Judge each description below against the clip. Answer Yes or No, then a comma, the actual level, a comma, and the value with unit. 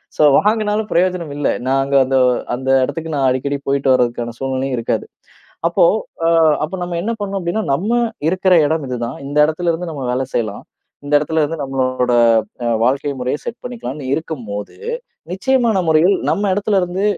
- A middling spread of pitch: No, wide, 6.0 semitones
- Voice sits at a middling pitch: Yes, medium, 155 Hz